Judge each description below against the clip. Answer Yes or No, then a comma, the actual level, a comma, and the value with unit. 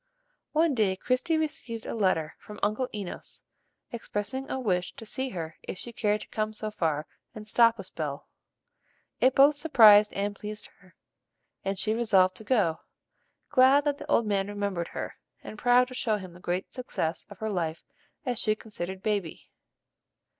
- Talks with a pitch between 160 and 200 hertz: No, high, 215 Hz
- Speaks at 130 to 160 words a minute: No, average, 175 wpm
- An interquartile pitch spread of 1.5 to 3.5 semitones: No, average, 4.5 semitones